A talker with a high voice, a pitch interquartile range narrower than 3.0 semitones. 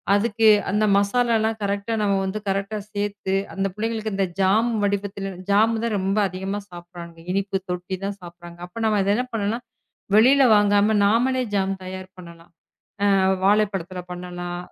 Yes: high, 200 Hz; narrow, 2.5 semitones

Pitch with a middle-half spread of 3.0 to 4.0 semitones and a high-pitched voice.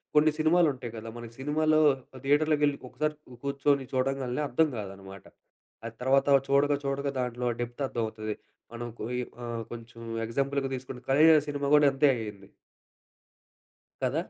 No: average, 3.5 semitones; low, 135 Hz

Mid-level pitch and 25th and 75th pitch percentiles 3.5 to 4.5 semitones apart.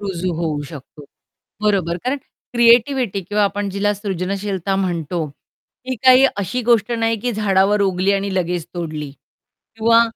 No: high, 200 Hz; average, 4.0 semitones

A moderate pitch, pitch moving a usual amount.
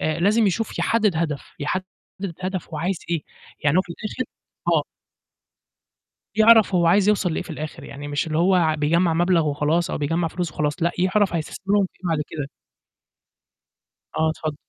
Yes: medium, 170 Hz; average, 3.5 semitones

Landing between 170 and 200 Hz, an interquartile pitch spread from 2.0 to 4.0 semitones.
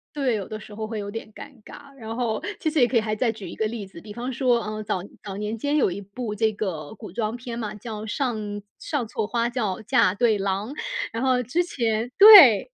No: high, 220 Hz; average, 2.8 semitones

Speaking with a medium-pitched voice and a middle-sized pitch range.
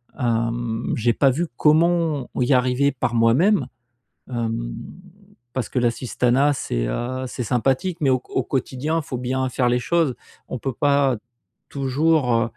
No: low, 130 Hz; average, 3.0 semitones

